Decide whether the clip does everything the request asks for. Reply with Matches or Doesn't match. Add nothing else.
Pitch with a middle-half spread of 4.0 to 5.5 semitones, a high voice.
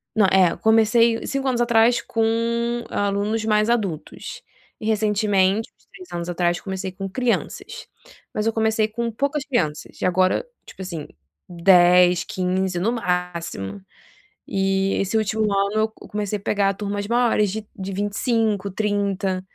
Doesn't match